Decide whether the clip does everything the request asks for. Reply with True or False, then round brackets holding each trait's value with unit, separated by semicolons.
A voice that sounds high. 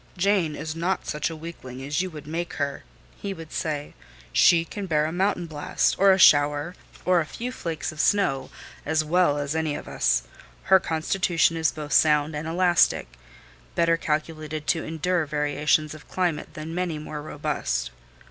False (155 Hz)